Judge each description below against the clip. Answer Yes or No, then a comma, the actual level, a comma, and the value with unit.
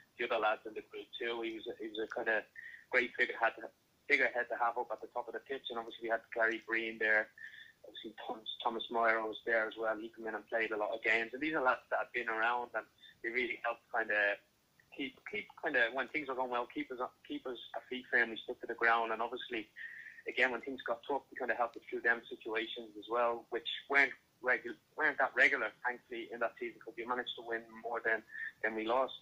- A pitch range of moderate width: No, narrow, 2.1 semitones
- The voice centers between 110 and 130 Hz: Yes, low, 115 Hz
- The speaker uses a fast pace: Yes, fast, 255 wpm